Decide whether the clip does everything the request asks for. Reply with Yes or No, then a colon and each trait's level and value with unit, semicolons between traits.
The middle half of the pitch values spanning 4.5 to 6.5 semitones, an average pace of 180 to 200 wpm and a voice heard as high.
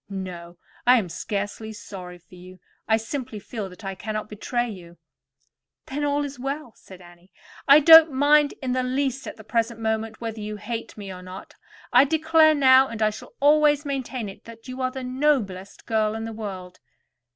Yes: average, 5.2 semitones; average, 190 wpm; high, 225 Hz